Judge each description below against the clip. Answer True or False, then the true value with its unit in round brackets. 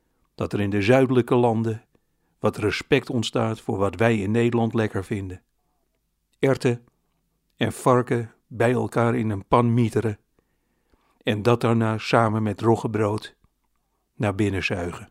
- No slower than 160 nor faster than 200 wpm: False (135 wpm)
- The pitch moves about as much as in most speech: False (2.2 semitones)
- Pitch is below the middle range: True (115 Hz)